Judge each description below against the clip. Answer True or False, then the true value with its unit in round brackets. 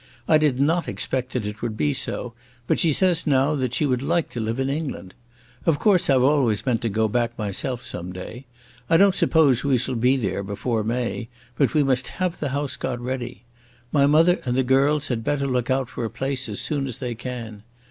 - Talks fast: True (220 wpm)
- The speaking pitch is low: True (130 Hz)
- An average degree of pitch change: True (3.5 semitones)